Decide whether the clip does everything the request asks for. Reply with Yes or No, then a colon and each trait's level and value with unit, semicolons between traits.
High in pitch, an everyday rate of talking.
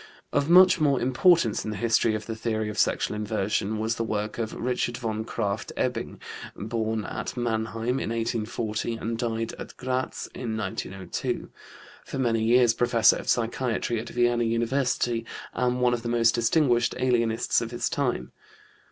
No: low, 115 Hz; average, 160 wpm